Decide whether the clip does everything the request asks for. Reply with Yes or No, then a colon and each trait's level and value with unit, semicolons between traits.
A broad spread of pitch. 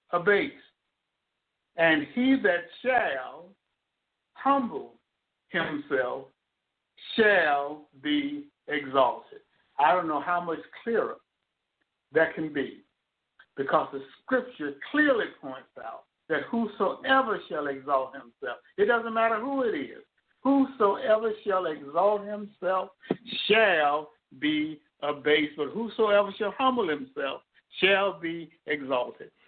Yes: wide, 7.7 semitones